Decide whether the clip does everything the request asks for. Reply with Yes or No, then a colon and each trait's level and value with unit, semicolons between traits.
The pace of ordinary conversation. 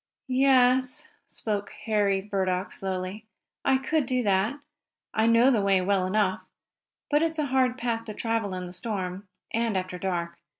Yes: average, 160 wpm